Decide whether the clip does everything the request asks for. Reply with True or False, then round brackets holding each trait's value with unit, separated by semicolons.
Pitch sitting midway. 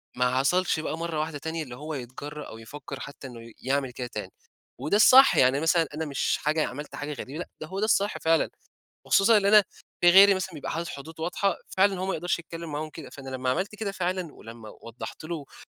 True (155 Hz)